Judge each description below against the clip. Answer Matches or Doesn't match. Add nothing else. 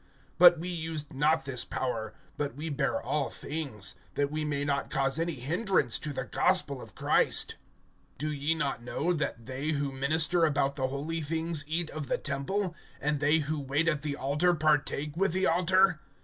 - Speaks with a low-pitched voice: Doesn't match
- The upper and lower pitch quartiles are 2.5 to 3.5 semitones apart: Matches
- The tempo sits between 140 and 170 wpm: Doesn't match